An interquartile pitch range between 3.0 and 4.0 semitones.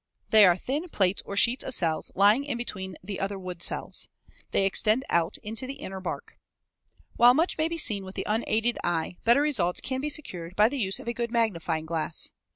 No: average, 5.1 semitones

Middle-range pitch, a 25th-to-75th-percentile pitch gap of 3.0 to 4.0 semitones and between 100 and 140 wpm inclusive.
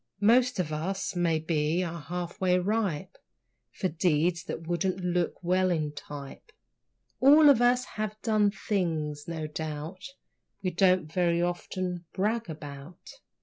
Yes: medium, 175 Hz; average, 3.4 semitones; slow, 135 wpm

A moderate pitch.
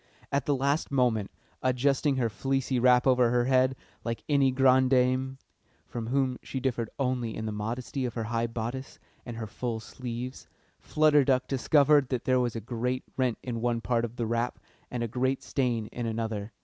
No: low, 125 Hz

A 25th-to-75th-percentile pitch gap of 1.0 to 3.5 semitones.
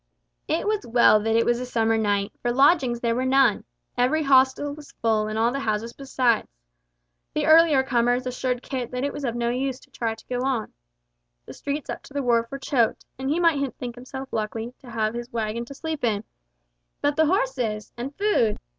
Yes: average, 3.0 semitones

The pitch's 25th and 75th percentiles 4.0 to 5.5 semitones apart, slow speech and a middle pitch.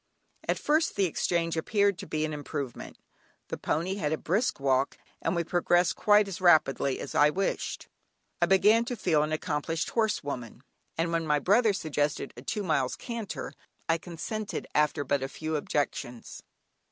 No: average, 5.0 semitones; average, 170 wpm; medium, 165 Hz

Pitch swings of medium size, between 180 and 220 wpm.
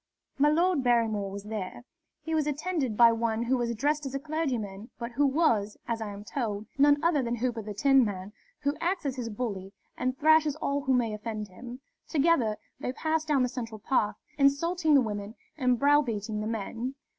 Yes: average, 5.0 semitones; average, 190 wpm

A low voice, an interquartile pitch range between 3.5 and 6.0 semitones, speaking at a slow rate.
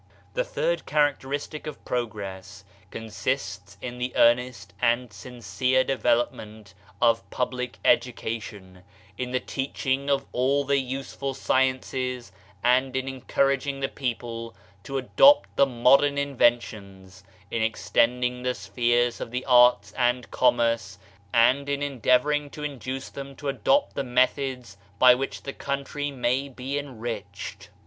No: low, 125 Hz; average, 2.9 semitones; slow, 130 wpm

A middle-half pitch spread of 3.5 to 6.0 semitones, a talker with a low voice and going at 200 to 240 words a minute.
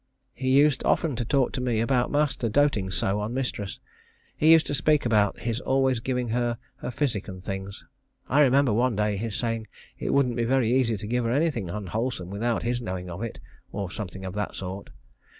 Yes: average, 4.2 semitones; low, 115 Hz; fast, 205 wpm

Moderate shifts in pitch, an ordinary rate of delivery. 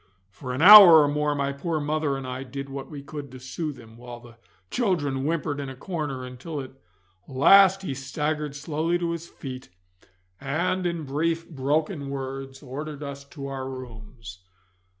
Yes: average, 3.0 semitones; average, 170 wpm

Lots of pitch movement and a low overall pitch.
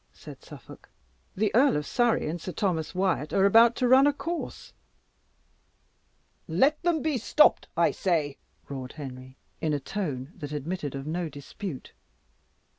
No: wide, 8.2 semitones; medium, 175 Hz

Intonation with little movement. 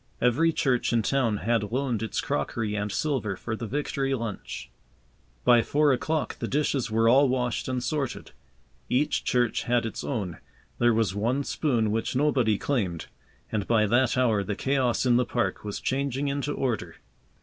No: average, 3.6 semitones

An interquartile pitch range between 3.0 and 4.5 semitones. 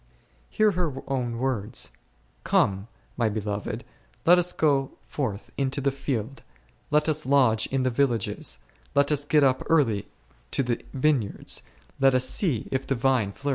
Yes: average, 3.5 semitones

